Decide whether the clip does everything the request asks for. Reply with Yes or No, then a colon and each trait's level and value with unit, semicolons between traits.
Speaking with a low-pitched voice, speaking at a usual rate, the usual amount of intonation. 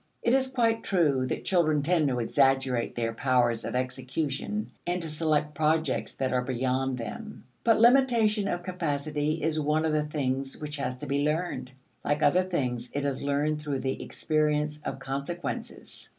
No: medium, 150 Hz; average, 170 wpm; average, 4.0 semitones